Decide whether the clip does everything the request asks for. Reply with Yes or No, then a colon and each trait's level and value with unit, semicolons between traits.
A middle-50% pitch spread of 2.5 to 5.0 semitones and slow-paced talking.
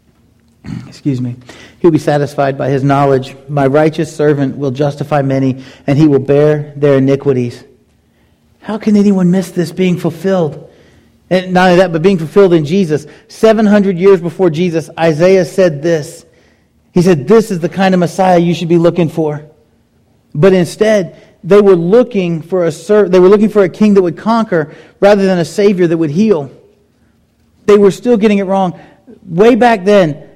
No: average, 4.7 semitones; average, 180 wpm